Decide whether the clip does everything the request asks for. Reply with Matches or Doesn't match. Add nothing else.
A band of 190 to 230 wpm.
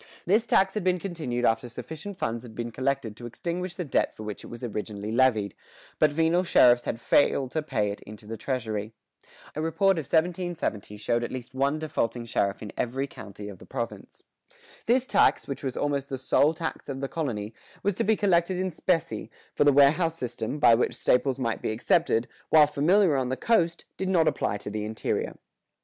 Matches